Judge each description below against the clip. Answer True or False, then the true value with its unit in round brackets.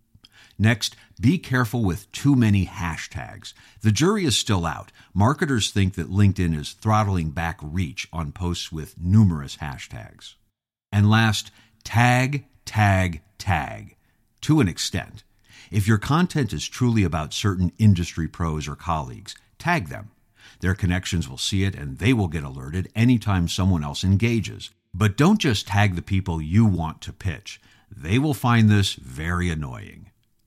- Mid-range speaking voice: False (105 Hz)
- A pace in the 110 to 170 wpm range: True (150 wpm)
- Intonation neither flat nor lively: True (4.2 semitones)